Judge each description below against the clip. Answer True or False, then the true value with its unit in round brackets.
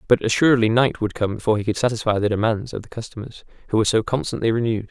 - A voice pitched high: False (110 Hz)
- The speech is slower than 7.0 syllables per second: False (7.6 syllables/s)